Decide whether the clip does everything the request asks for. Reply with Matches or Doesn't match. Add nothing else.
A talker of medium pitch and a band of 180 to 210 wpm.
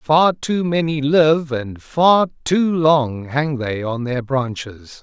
Doesn't match